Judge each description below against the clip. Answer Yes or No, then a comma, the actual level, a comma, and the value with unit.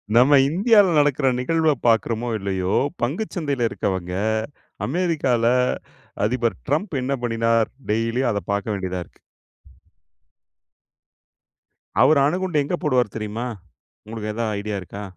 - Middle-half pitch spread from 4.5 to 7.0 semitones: Yes, wide, 5.6 semitones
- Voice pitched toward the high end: No, low, 120 Hz